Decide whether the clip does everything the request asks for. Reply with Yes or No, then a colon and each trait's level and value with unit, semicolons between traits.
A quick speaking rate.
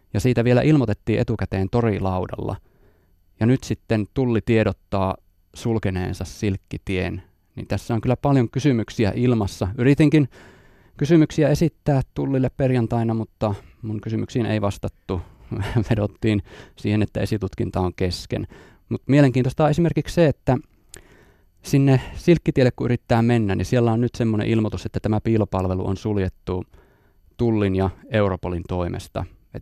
No: average, 125 wpm